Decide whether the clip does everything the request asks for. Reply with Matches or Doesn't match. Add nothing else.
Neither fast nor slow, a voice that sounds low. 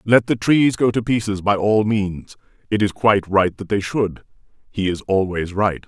Matches